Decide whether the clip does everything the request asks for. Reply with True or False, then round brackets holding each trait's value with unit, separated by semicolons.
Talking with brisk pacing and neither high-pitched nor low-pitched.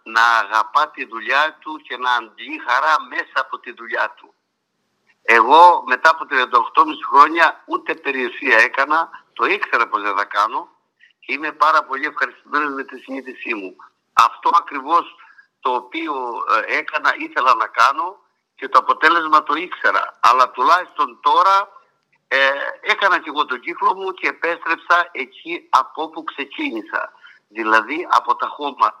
False (145 wpm; 175 Hz)